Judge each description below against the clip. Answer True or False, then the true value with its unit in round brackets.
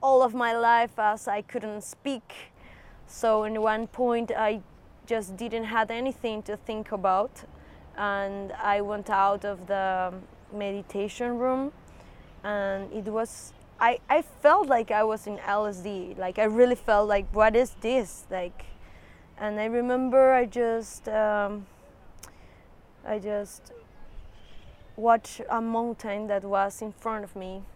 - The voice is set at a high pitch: True (215 Hz)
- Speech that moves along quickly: False (140 wpm)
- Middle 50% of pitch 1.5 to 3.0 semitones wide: True (2.6 semitones)